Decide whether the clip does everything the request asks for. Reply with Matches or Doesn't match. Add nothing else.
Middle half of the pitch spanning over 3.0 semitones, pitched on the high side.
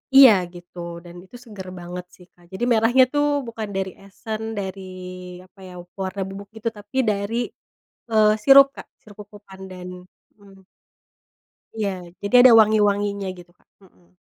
Doesn't match